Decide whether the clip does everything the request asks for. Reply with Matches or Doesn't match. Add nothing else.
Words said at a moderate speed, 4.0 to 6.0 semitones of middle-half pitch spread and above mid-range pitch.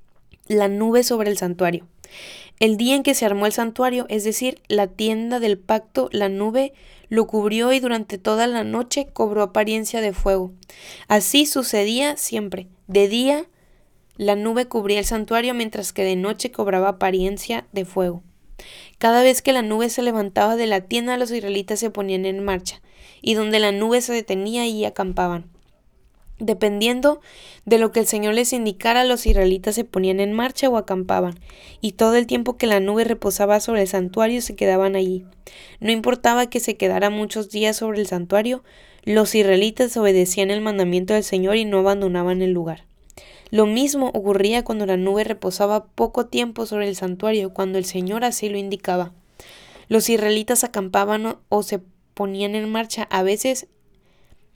Doesn't match